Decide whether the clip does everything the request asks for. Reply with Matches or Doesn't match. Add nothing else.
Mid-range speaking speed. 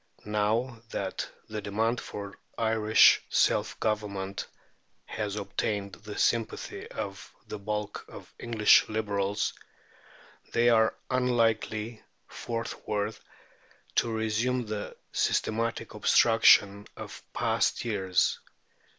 Doesn't match